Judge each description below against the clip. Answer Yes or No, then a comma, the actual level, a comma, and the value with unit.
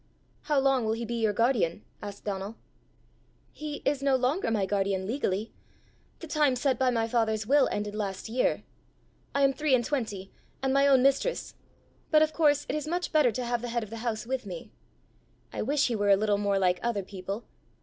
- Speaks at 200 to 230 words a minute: Yes, fast, 205 wpm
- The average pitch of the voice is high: Yes, high, 235 Hz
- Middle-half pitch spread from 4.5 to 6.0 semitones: Yes, average, 4.9 semitones